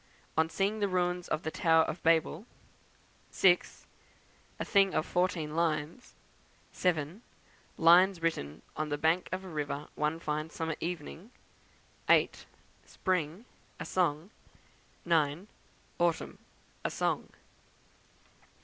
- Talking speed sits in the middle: No, slow, 115 wpm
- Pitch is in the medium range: Yes, medium, 165 Hz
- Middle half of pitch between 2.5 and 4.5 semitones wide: Yes, average, 3.0 semitones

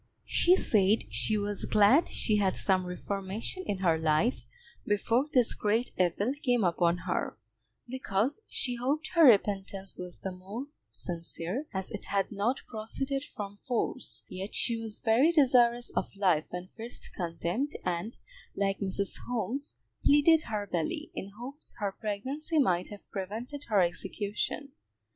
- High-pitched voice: Yes, high, 210 Hz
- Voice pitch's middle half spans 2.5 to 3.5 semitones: No, average, 4.7 semitones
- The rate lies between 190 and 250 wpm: No, average, 145 wpm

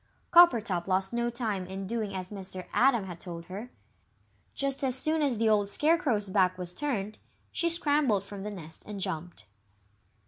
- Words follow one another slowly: No, average, 170 wpm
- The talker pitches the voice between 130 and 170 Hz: No, high, 210 Hz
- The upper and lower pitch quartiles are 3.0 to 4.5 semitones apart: No, wide, 5.5 semitones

